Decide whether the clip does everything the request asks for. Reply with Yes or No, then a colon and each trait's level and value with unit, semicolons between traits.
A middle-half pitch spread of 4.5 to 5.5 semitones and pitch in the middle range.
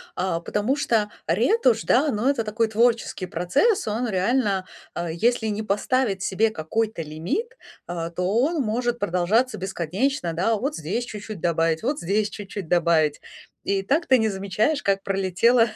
No: average, 5.0 semitones; high, 210 Hz